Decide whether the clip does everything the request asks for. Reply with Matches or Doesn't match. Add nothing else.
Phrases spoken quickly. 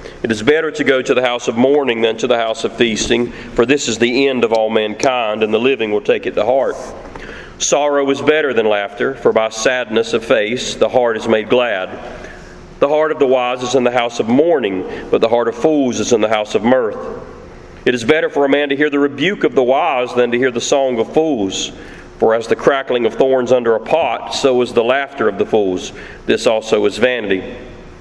Matches